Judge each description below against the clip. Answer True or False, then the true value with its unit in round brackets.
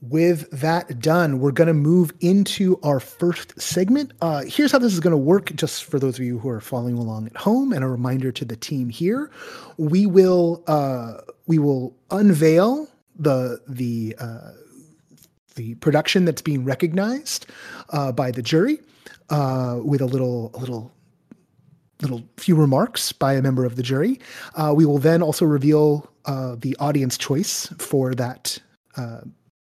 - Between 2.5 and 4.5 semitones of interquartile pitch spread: False (5.2 semitones)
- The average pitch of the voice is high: False (145 Hz)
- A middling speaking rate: True (170 wpm)